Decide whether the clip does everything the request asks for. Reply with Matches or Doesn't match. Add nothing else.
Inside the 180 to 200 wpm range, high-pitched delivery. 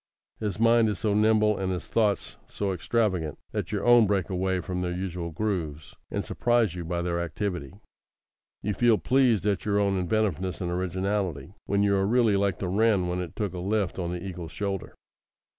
Doesn't match